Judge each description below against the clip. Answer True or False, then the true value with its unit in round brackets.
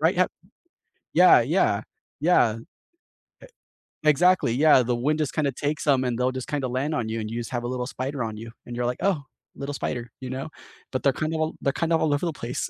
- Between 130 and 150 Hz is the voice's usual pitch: True (135 Hz)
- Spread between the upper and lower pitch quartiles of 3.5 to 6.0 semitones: True (3.9 semitones)